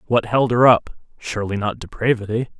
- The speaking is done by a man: Yes, male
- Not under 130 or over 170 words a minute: Yes, average, 140 wpm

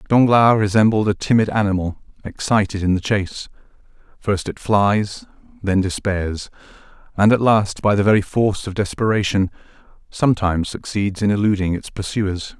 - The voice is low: Yes, low, 100 Hz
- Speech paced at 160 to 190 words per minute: No, average, 140 wpm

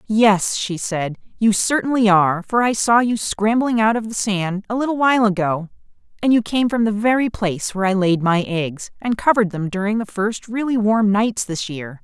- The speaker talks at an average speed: No, fast, 210 wpm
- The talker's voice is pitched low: No, high, 210 Hz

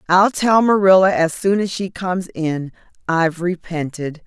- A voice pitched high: No, medium, 180 Hz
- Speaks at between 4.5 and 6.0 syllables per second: Yes, 4.6 syllables/s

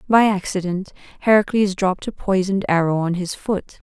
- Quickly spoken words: No, average, 155 wpm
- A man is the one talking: No, female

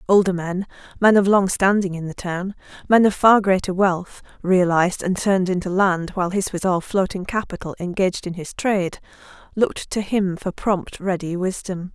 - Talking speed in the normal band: Yes, average, 170 wpm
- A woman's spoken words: Yes, female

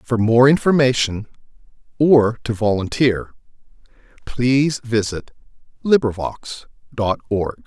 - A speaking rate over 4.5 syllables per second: No, 3.9 syllables/s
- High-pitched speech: No, low, 120 Hz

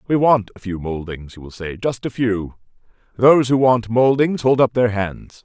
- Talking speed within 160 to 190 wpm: No, average, 200 wpm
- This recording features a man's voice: Yes, male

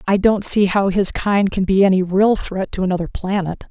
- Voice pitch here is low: No, high, 195 Hz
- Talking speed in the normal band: No, fast, 225 wpm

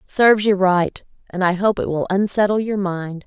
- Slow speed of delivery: No, average, 200 wpm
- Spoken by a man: No, female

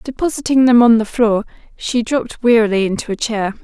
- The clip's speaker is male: No, female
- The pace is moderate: Yes, average, 180 wpm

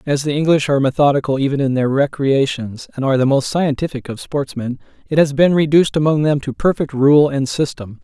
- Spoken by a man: Yes, male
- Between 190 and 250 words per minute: Yes, average, 200 wpm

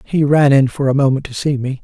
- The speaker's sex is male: Yes, male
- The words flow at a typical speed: No, fast, 295 wpm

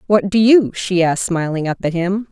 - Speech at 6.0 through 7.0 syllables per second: No, 5.3 syllables/s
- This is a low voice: No, high, 190 Hz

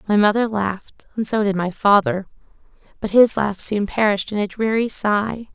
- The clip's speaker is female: Yes, female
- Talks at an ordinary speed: Yes, average, 185 wpm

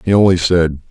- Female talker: No, male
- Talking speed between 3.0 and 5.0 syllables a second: No, 5.5 syllables/s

